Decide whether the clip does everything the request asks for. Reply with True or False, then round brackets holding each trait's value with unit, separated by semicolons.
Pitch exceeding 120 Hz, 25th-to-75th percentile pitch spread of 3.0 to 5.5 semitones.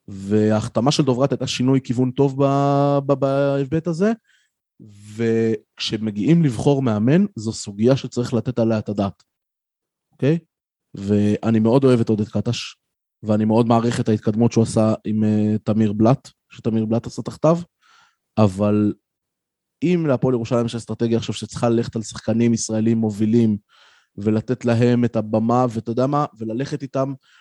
False (115 Hz; 3.5 semitones)